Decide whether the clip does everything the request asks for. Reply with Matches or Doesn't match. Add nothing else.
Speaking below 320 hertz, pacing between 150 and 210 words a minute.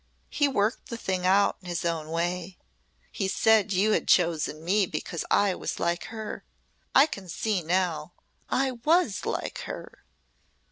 Matches